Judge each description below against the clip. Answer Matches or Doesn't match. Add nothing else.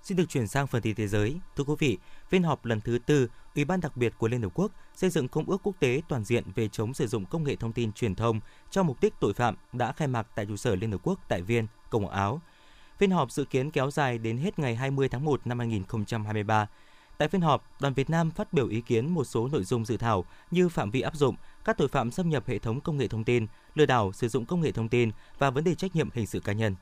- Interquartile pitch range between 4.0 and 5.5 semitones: Matches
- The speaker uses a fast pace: Matches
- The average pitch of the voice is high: Doesn't match